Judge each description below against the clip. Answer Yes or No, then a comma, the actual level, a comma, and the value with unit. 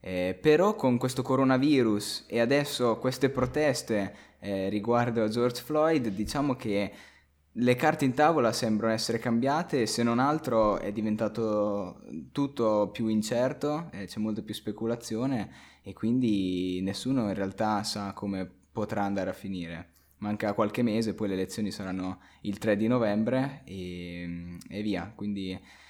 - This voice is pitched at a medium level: No, low, 105 Hz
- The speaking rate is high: No, average, 145 wpm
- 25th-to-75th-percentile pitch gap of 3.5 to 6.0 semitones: Yes, average, 4.2 semitones